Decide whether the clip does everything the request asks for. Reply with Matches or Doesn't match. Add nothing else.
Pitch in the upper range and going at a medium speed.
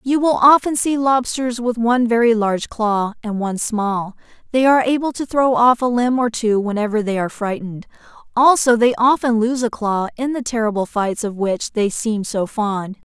Matches